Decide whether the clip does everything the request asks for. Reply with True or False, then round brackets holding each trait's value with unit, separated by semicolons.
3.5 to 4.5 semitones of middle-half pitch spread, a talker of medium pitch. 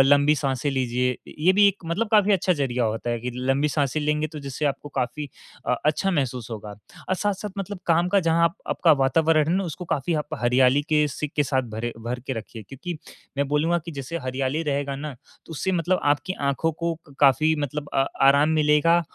True (3.9 semitones; 150 Hz)